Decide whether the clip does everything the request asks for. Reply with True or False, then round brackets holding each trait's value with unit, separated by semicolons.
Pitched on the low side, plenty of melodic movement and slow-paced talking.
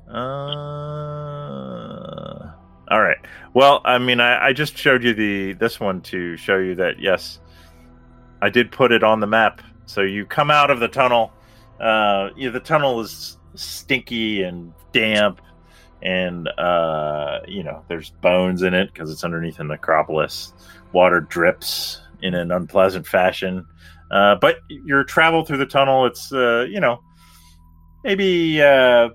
False (100 Hz; 6.3 semitones; 150 wpm)